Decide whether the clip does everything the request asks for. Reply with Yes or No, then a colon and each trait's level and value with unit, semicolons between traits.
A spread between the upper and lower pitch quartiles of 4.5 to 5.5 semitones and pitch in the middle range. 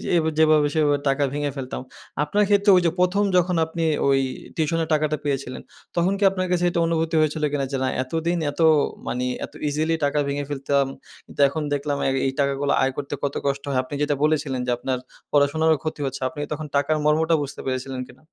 No: narrow, 2.6 semitones; medium, 145 Hz